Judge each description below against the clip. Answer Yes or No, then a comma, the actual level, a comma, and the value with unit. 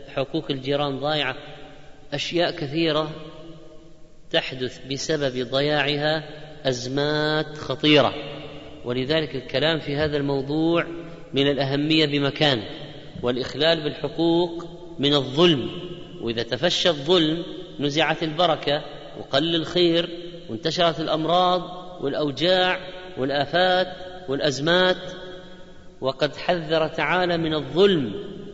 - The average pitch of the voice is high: No, medium, 155 Hz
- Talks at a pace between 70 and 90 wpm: Yes, average, 80 wpm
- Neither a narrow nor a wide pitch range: Yes, average, 3.0 semitones